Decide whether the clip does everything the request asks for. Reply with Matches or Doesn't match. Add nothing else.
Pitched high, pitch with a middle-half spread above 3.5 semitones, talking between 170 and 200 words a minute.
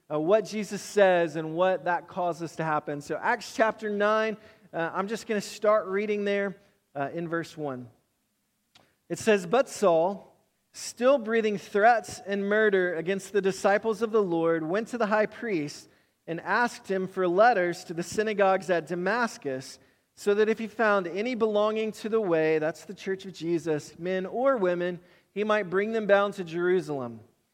Matches